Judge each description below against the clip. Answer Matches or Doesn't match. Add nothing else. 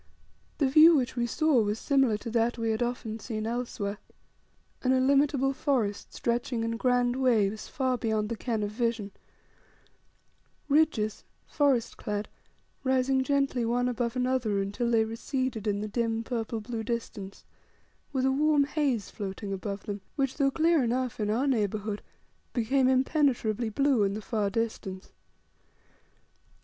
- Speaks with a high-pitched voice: Matches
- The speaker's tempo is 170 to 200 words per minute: Doesn't match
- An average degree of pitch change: Matches